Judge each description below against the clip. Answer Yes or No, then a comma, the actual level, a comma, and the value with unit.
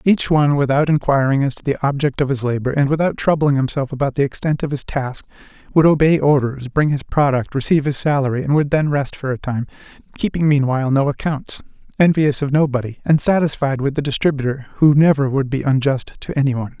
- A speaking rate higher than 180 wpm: Yes, fast, 205 wpm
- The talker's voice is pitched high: No, medium, 140 Hz